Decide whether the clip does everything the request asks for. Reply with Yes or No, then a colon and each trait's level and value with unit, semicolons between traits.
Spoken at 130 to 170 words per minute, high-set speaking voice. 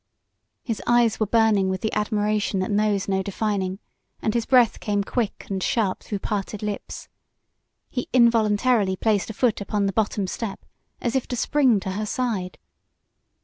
Yes: average, 165 wpm; high, 210 Hz